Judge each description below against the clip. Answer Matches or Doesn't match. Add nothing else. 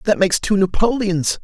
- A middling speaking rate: Matches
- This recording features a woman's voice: Doesn't match